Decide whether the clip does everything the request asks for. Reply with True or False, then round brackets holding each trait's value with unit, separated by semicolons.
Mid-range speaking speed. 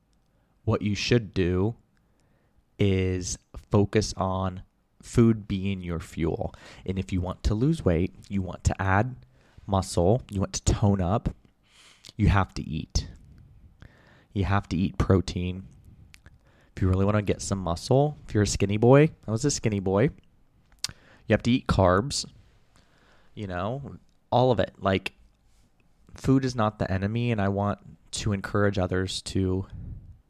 True (155 wpm)